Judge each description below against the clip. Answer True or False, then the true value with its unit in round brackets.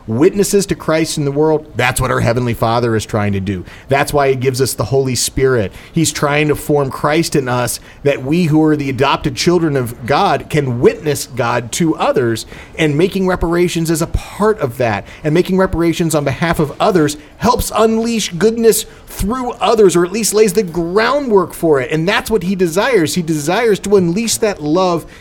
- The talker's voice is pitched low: False (155 Hz)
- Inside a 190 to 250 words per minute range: True (200 wpm)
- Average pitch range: False (5.7 semitones)